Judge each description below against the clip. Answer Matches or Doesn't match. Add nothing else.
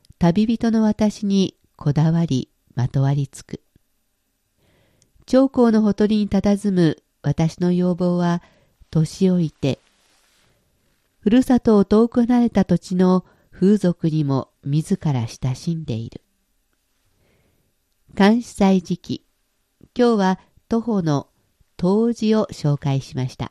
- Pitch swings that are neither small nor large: Doesn't match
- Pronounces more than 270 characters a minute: Doesn't match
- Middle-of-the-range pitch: Matches